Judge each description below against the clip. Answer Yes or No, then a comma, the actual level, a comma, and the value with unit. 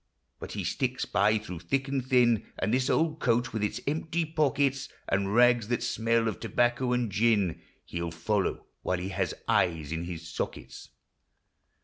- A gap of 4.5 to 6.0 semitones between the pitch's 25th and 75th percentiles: Yes, average, 5.3 semitones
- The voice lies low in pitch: Yes, low, 115 Hz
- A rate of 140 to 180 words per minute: Yes, average, 170 wpm